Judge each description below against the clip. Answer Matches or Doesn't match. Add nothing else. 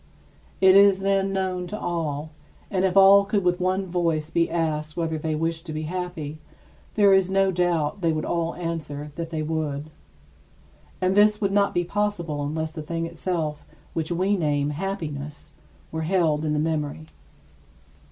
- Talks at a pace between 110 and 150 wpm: Doesn't match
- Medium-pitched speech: Matches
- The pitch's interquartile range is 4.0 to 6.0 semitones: Doesn't match